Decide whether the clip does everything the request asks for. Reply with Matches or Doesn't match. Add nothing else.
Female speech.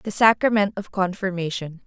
Matches